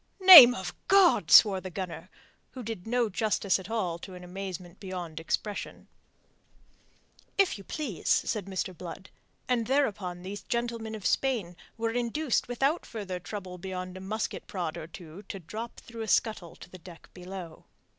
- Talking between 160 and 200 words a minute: Yes, average, 165 wpm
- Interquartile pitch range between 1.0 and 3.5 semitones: No, average, 4.1 semitones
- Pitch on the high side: Yes, high, 195 Hz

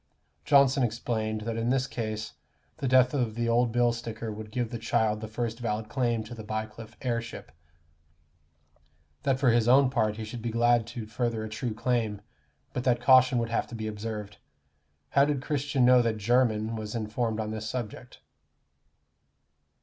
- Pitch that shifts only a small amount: Yes, narrow, 2.2 semitones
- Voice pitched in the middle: No, low, 115 Hz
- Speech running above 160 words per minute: Yes, average, 175 wpm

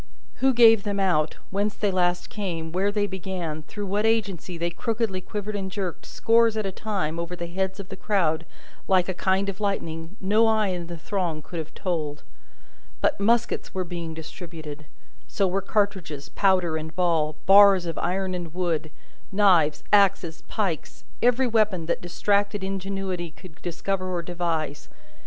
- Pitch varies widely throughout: No, average, 3.1 semitones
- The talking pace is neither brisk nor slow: Yes, average, 165 wpm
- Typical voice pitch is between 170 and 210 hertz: Yes, medium, 185 Hz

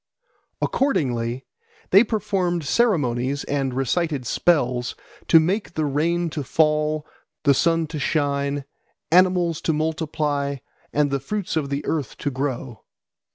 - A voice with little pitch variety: No, average, 3.5 semitones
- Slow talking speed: Yes, slow, 125 wpm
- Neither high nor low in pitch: Yes, medium, 150 Hz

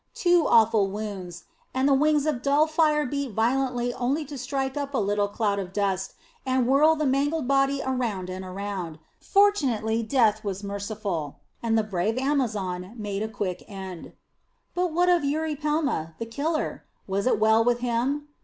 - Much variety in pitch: Yes, wide, 5.7 semitones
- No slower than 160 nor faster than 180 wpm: Yes, average, 165 wpm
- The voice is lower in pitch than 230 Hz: No, high, 240 Hz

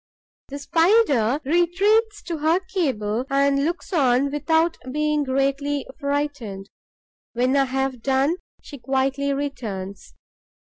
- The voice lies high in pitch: Yes, very high, 280 Hz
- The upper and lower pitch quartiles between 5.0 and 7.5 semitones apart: No, average, 3.3 semitones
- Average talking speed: No, slow, 110 wpm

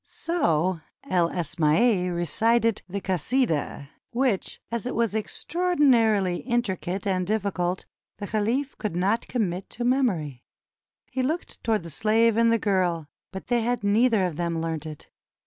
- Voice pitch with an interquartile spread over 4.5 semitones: Yes, average, 5.0 semitones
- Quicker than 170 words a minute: No, average, 145 wpm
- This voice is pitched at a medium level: No, high, 205 Hz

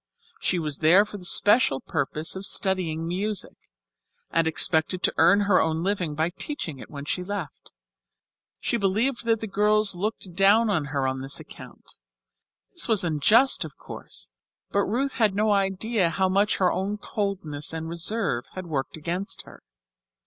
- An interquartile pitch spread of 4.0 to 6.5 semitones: Yes, average, 4.3 semitones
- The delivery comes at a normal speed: Yes, average, 165 wpm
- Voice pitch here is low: No, high, 190 Hz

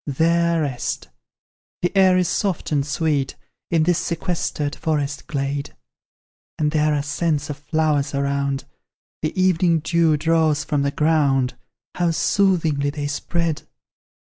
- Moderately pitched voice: Yes, medium, 155 Hz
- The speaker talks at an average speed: No, slow, 130 wpm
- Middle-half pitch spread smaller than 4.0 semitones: Yes, average, 2.8 semitones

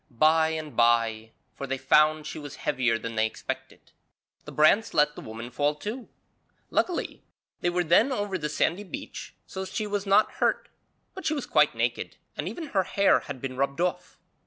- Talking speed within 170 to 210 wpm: Yes, average, 185 wpm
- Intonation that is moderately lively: No, wide, 6.9 semitones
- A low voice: No, medium, 155 Hz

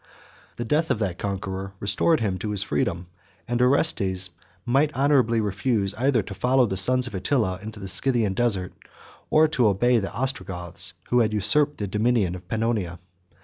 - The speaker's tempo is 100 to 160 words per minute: No, average, 170 wpm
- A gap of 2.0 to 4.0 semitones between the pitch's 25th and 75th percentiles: No, average, 4.6 semitones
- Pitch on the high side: No, low, 110 Hz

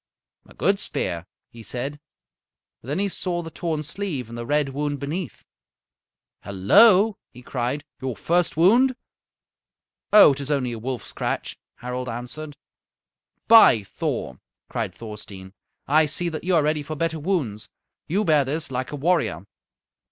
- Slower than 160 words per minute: Yes, average, 150 wpm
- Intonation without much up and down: No, wide, 5.4 semitones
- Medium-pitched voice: Yes, medium, 145 Hz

